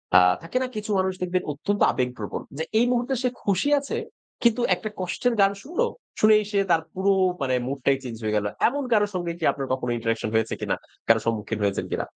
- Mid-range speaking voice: Yes, medium, 180 Hz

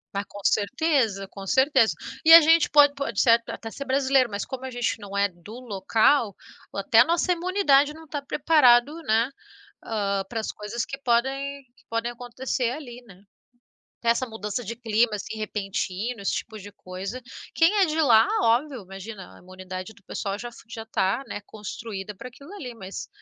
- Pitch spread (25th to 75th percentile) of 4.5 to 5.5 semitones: Yes, average, 5.1 semitones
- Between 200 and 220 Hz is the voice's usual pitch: No, high, 235 Hz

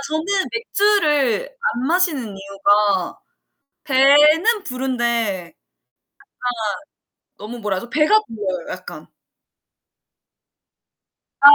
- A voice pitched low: No, very high, 250 Hz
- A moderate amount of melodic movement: No, wide, 7.2 semitones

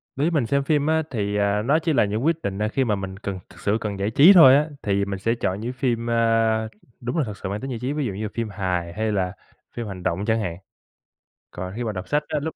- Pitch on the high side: No, low, 110 Hz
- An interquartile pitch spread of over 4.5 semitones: Yes, average, 5.1 semitones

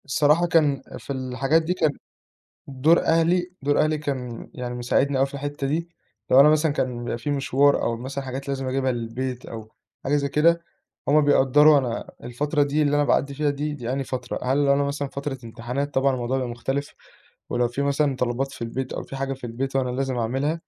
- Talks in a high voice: No, low, 135 Hz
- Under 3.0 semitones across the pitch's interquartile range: Yes, narrow, 2.4 semitones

